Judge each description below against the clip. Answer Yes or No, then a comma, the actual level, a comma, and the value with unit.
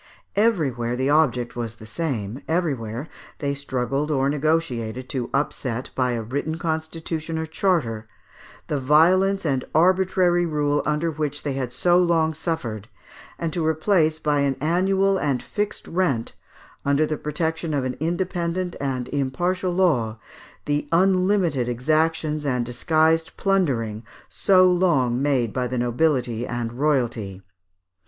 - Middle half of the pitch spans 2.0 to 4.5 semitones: No, average, 4.9 semitones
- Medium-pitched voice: Yes, medium, 150 Hz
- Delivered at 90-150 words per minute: Yes, slow, 135 wpm